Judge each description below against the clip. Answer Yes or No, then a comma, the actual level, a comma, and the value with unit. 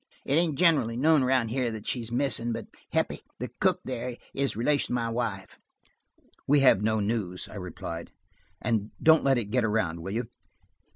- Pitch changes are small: No, average, 3.8 semitones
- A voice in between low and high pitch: No, low, 115 Hz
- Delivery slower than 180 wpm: No, average, 185 wpm